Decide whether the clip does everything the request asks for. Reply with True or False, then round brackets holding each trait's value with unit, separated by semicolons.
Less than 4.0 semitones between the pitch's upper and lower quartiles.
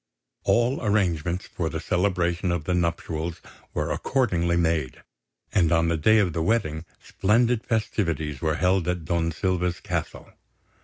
True (3.3 semitones)